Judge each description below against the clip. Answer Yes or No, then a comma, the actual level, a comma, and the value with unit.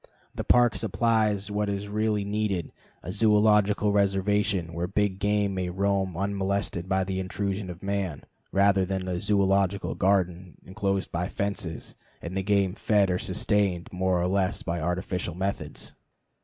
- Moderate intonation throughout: No, narrow, 1.9 semitones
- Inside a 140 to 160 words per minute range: Yes, average, 150 wpm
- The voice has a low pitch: Yes, low, 100 Hz